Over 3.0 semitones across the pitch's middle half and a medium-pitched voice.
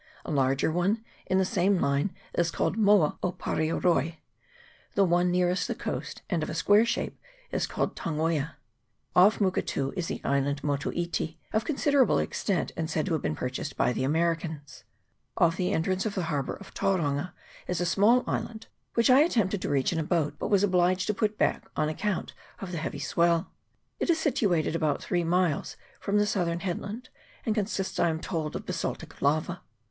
Yes: average, 4.0 semitones; medium, 175 Hz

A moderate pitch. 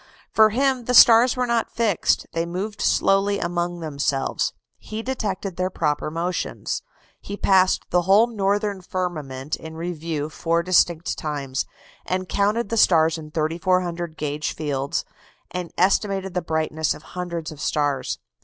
Yes: medium, 175 Hz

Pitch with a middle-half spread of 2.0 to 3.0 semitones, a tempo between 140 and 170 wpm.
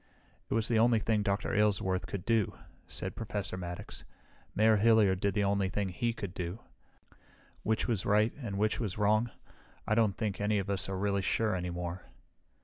No: narrow, 2.4 semitones; average, 185 wpm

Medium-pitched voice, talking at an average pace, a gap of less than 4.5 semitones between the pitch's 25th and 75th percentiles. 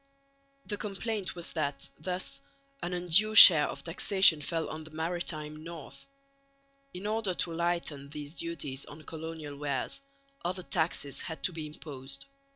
Yes: medium, 165 Hz; average, 145 wpm; average, 3.1 semitones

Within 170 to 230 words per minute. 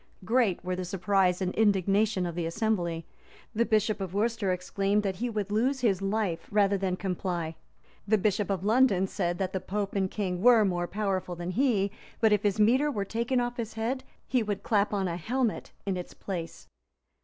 Yes: average, 195 wpm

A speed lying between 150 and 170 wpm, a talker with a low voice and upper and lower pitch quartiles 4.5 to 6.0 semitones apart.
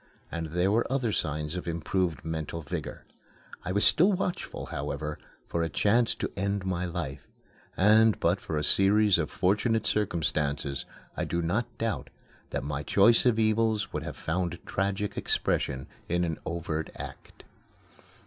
Yes: average, 155 wpm; very low, 90 Hz; average, 5.0 semitones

